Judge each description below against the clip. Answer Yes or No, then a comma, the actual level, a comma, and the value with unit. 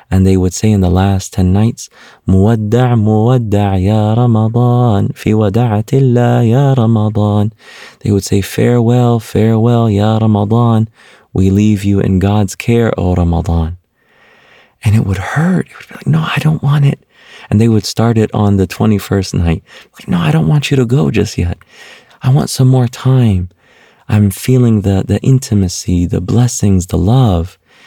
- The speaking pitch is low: Yes, low, 110 Hz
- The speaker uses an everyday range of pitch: Yes, average, 3.7 semitones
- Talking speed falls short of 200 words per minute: Yes, average, 170 wpm